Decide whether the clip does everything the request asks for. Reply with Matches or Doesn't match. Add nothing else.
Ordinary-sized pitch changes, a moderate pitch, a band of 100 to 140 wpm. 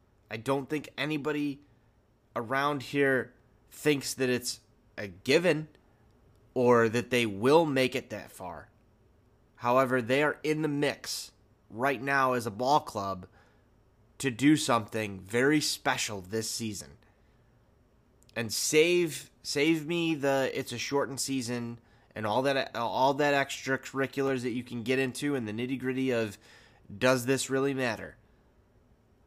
Doesn't match